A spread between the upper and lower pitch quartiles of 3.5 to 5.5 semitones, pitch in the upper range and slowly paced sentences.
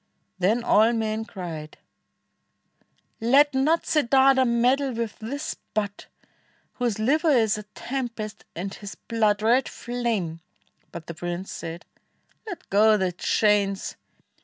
Yes: average, 4.1 semitones; high, 220 Hz; slow, 120 wpm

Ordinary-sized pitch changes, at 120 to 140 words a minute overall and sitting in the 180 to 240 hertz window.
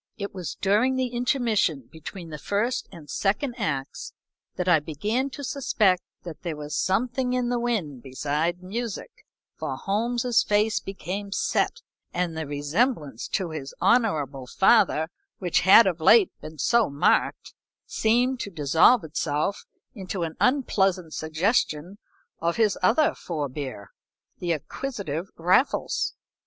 No: wide, 6.8 semitones; slow, 135 wpm; high, 190 Hz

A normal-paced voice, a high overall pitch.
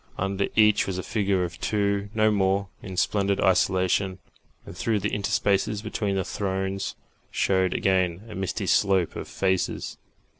No: average, 150 wpm; very low, 95 Hz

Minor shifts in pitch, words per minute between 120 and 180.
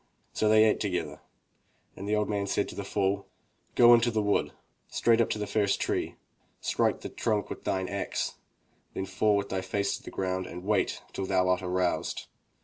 No: narrow, 2.2 semitones; average, 200 wpm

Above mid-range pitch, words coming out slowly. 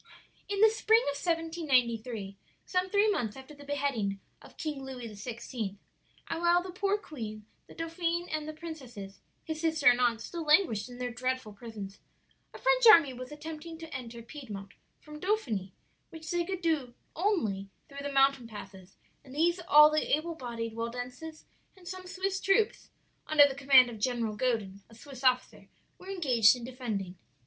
No: very high, 275 Hz; average, 170 wpm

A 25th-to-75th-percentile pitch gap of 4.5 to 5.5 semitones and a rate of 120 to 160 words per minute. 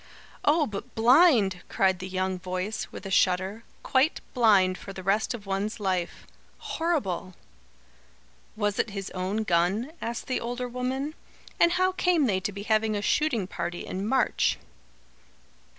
Yes: average, 5.0 semitones; average, 150 wpm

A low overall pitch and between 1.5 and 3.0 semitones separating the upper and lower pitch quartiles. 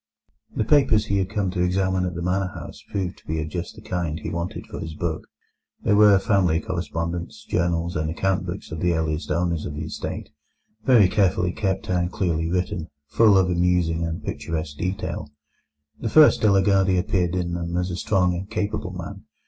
Yes: very low, 90 Hz; narrow, 2.4 semitones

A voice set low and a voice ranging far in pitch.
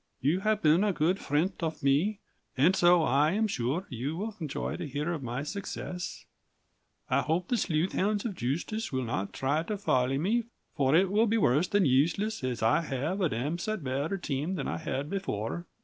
No: medium, 165 Hz; wide, 6.1 semitones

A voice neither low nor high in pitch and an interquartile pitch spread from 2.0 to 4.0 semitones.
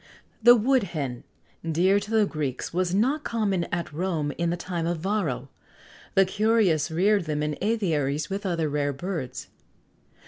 No: medium, 175 Hz; average, 5.0 semitones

